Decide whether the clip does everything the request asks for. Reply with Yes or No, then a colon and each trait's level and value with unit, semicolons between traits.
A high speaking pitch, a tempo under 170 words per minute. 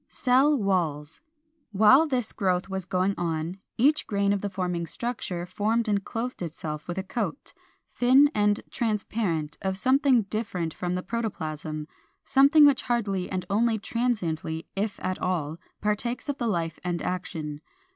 Yes: high, 200 Hz; average, 155 wpm